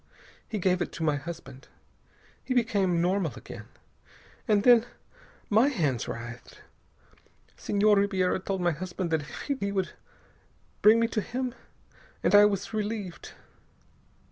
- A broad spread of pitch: No, average, 3.8 semitones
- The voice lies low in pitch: No, high, 195 Hz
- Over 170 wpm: No, slow, 135 wpm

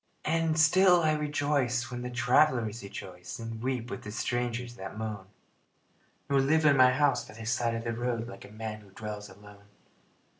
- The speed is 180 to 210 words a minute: Yes, average, 185 wpm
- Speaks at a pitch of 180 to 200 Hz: No, low, 120 Hz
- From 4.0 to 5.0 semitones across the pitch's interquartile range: Yes, average, 4.4 semitones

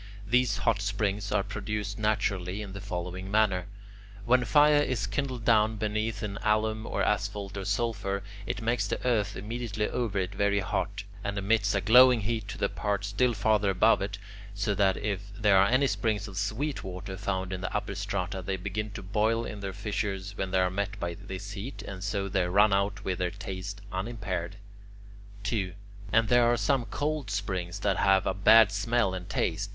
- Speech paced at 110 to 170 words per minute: No, average, 190 wpm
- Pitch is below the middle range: Yes, low, 100 Hz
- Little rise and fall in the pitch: Yes, narrow, 2.1 semitones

